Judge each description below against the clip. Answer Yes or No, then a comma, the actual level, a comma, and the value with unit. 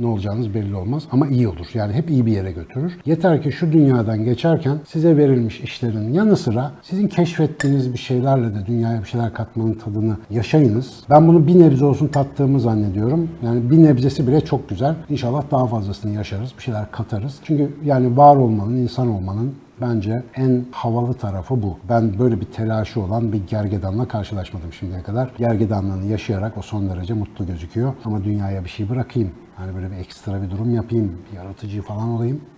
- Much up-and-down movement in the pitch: No, average, 4.4 semitones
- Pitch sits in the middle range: No, low, 115 Hz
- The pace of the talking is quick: Yes, fast, 180 wpm